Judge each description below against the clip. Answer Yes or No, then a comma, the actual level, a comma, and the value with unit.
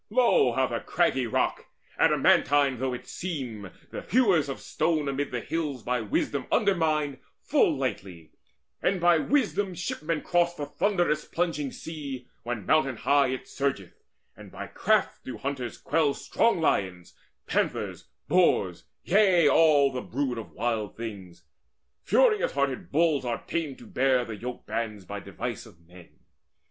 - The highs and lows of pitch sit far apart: Yes, wide, 5.7 semitones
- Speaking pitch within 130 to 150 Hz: Yes, medium, 140 Hz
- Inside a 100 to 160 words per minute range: Yes, average, 150 wpm